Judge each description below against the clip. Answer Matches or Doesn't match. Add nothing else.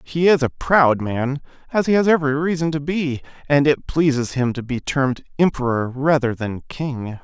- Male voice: Matches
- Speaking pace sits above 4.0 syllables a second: Matches